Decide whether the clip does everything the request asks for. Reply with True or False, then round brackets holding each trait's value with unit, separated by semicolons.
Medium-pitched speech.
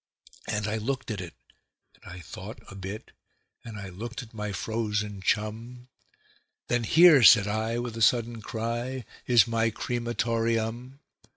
False (115 Hz)